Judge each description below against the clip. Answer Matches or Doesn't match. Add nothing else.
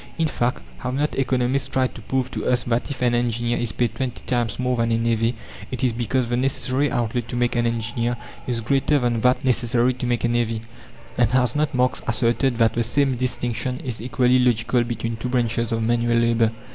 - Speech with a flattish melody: Matches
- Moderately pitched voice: Doesn't match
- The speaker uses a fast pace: Matches